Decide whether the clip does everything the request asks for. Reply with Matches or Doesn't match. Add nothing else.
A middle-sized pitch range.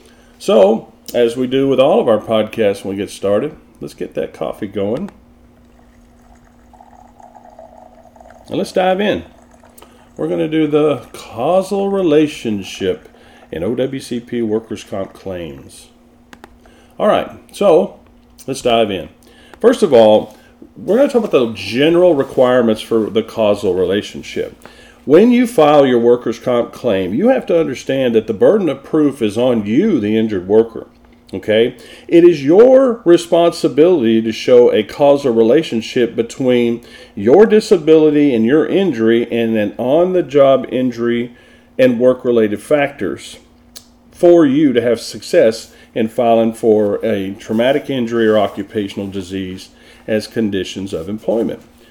Doesn't match